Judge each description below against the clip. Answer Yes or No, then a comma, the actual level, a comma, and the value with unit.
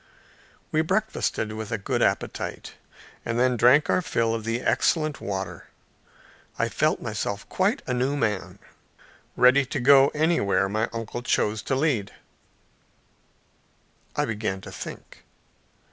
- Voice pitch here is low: Yes, low, 120 Hz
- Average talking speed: No, slow, 130 wpm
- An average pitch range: Yes, average, 4.9 semitones